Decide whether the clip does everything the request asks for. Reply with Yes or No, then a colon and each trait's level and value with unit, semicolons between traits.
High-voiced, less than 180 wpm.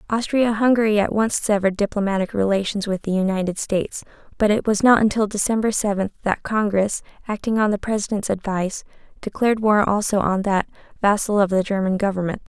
Yes: high, 205 Hz; average, 165 wpm